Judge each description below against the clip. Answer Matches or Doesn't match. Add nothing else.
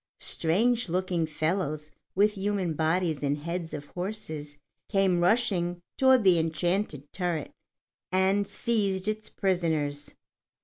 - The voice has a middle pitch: Matches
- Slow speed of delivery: Matches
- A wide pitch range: Doesn't match